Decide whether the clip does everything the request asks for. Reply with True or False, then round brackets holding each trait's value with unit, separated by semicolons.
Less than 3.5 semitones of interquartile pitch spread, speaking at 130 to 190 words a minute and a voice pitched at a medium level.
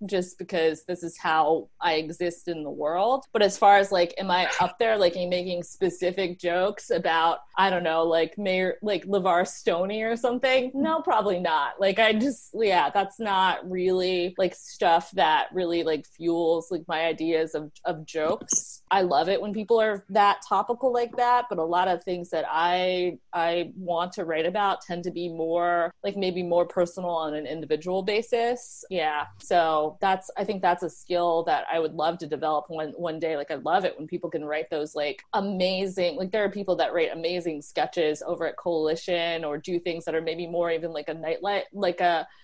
False (3.0 semitones; 200 wpm; 175 Hz)